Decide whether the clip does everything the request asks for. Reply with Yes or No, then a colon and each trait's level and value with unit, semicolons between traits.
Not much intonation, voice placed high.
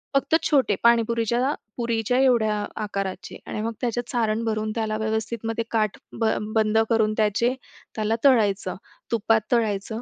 Yes: narrow, 1.6 semitones; high, 225 Hz